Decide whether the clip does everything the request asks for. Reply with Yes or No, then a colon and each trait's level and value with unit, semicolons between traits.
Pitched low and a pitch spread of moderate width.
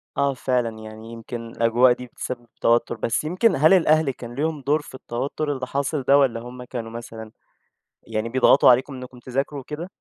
Yes: low, 125 Hz; average, 3.3 semitones